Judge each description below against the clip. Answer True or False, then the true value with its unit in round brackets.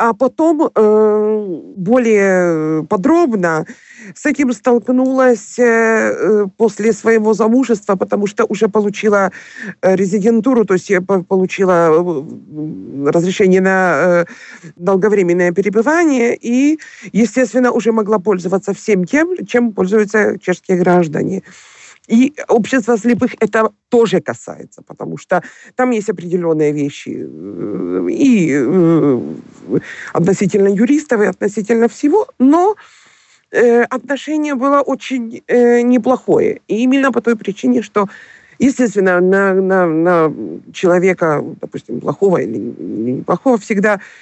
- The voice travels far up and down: False (4.7 semitones)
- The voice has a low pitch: False (215 Hz)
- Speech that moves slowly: True (100 wpm)